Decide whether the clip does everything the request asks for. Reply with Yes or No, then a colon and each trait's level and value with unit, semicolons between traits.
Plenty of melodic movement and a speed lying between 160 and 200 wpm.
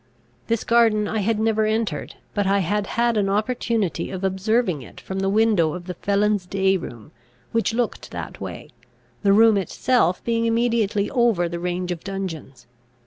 No: average, 3.5 semitones; average, 170 wpm